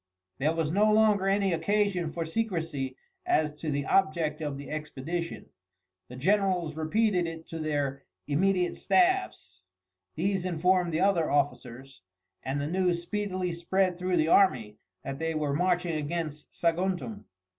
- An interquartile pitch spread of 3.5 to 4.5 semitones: Yes, average, 4.0 semitones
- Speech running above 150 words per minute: No, average, 145 wpm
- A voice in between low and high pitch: Yes, medium, 165 Hz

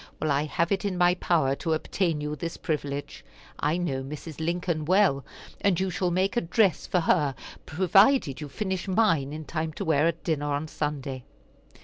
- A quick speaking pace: No, average, 190 wpm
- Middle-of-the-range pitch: Yes, medium, 160 Hz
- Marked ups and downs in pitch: No, average, 3.6 semitones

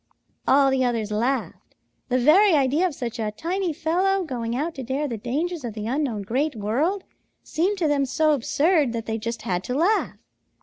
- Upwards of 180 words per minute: Yes, average, 190 wpm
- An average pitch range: No, wide, 5.7 semitones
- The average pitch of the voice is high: Yes, very high, 275 Hz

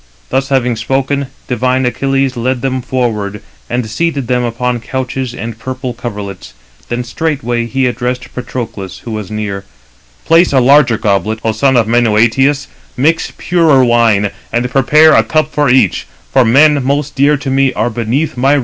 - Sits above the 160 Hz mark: No, low, 125 Hz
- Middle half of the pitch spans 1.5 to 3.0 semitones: Yes, average, 2.7 semitones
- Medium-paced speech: Yes, average, 165 wpm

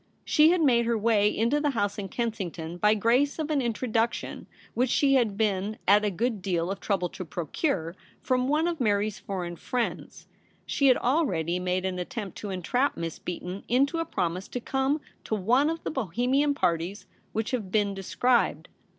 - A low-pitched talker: No, high, 220 Hz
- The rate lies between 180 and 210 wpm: Yes, average, 185 wpm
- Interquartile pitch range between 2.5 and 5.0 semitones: No, wide, 5.5 semitones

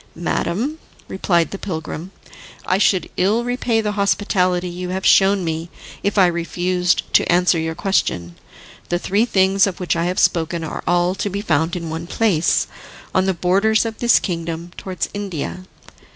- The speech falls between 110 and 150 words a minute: No, average, 165 wpm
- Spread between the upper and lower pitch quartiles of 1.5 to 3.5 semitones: Yes, average, 2.7 semitones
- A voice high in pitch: No, medium, 180 Hz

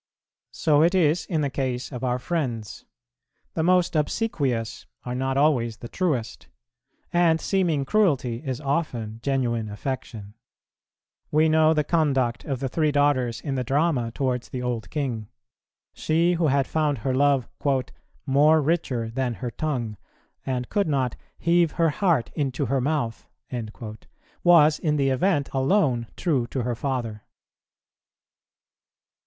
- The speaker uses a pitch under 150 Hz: Yes, medium, 140 Hz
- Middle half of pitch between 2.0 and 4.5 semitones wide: Yes, average, 4.2 semitones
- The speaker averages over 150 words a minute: No, average, 140 wpm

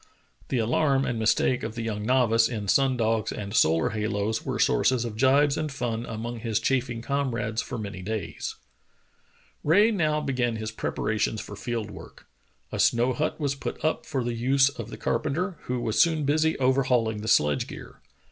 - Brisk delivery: No, average, 185 wpm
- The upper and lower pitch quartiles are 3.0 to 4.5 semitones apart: Yes, average, 3.7 semitones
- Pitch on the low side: Yes, low, 120 Hz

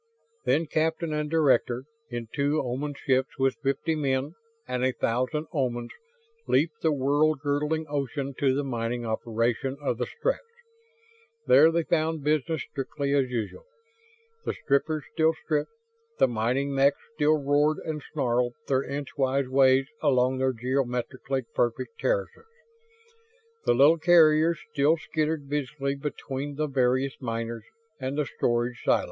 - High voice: No, medium, 140 Hz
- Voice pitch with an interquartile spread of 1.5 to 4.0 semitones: Yes, average, 3.1 semitones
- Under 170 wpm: Yes, average, 140 wpm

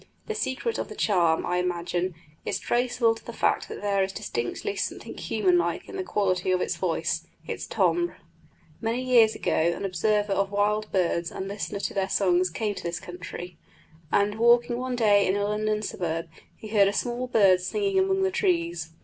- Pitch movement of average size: Yes, average, 4.7 semitones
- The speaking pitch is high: Yes, high, 205 Hz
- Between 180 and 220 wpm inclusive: Yes, average, 190 wpm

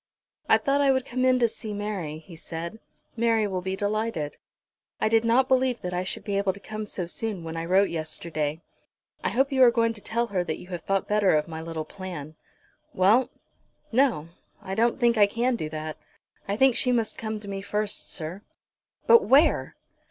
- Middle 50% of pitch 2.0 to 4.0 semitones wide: No, average, 5.3 semitones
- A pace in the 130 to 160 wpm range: No, fast, 205 wpm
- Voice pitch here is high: Yes, high, 205 Hz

